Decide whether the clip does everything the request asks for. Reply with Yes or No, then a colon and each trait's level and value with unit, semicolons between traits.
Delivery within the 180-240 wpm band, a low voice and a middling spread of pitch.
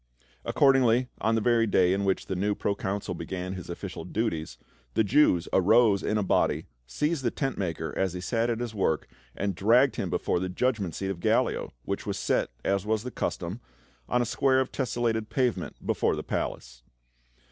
Yes: average, 190 wpm; low, 105 Hz; average, 4.5 semitones